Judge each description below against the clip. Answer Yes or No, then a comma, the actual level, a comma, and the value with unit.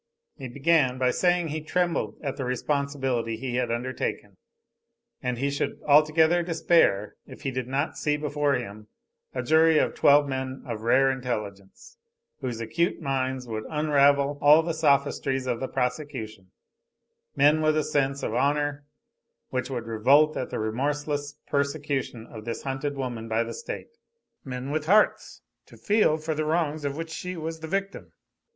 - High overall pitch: No, medium, 140 Hz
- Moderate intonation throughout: Yes, average, 3.5 semitones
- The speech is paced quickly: No, average, 165 wpm